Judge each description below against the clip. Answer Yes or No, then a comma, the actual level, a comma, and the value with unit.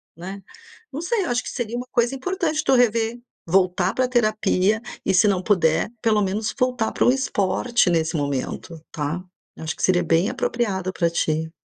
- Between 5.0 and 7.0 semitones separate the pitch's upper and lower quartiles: Yes, wide, 5.5 semitones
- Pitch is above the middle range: Yes, high, 205 Hz